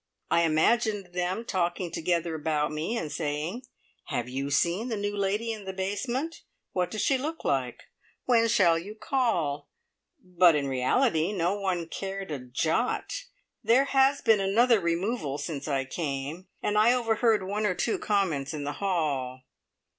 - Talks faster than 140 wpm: Yes, average, 160 wpm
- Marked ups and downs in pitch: Yes, wide, 6.2 semitones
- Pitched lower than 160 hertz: No, medium, 185 Hz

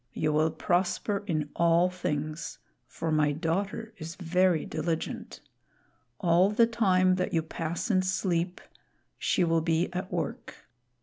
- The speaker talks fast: No, slow, 135 wpm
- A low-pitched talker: No, medium, 170 Hz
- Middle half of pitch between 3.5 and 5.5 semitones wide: No, narrow, 2.4 semitones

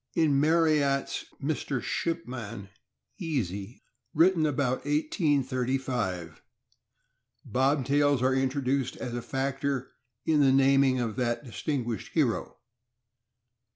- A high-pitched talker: No, low, 135 Hz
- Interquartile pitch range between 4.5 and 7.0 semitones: No, average, 2.8 semitones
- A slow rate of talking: Yes, slow, 90 wpm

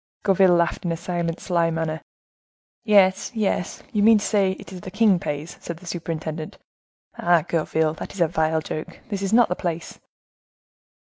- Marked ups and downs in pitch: No, average, 3.1 semitones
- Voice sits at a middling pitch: Yes, medium, 175 Hz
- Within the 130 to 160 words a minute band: No, average, 180 wpm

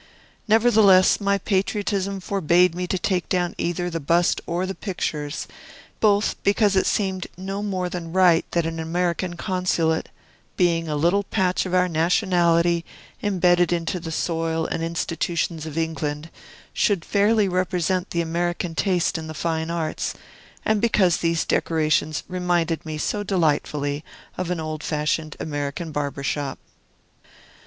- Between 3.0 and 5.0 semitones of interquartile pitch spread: No, narrow, 2.5 semitones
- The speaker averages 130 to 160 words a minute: Yes, average, 145 wpm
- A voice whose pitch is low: No, medium, 175 Hz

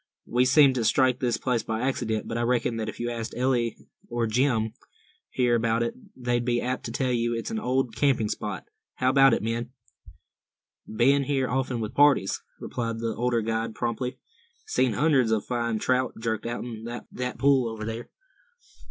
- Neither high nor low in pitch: No, low, 120 Hz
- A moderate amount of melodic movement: No, narrow, 2.1 semitones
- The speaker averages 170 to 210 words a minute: Yes, average, 180 wpm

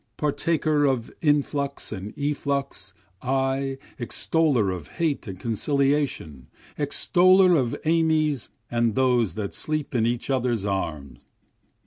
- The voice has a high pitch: No, low, 135 Hz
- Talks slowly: Yes, slow, 110 wpm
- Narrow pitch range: No, average, 4.9 semitones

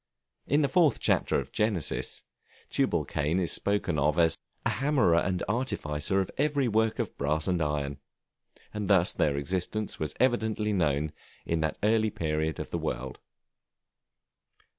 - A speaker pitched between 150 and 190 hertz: No, very low, 90 Hz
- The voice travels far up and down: Yes, wide, 6.1 semitones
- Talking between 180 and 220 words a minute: No, average, 145 wpm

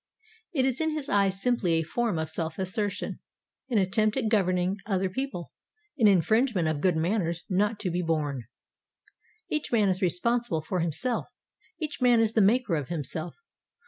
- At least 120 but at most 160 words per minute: No, average, 170 wpm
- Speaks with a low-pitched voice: No, high, 195 Hz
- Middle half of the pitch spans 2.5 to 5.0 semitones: No, wide, 5.4 semitones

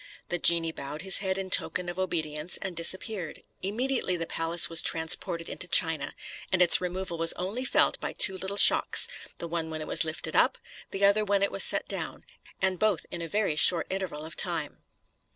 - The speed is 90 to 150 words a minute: No, average, 200 wpm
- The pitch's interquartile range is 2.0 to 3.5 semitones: Yes, average, 2.7 semitones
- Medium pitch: Yes, medium, 175 Hz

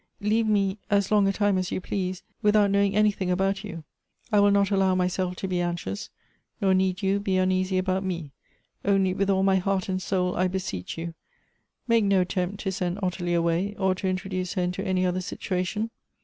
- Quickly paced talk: Yes, fast, 215 wpm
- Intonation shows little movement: Yes, narrow, 1.6 semitones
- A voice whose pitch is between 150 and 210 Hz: Yes, high, 190 Hz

